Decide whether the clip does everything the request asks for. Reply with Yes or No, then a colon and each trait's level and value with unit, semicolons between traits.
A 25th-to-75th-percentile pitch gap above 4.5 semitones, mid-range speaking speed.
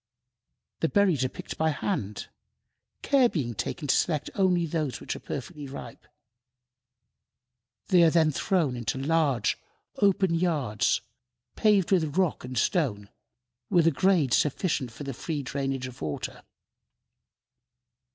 No: average, 5.2 semitones; slow, 130 wpm